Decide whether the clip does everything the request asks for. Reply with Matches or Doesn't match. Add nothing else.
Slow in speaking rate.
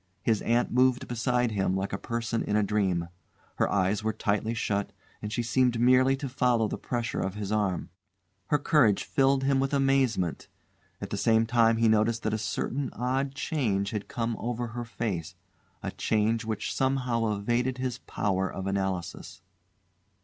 Doesn't match